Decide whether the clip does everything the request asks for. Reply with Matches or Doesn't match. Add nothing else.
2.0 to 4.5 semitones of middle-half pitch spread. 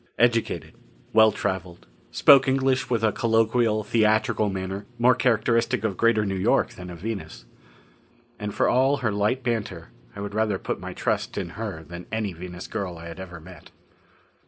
Matches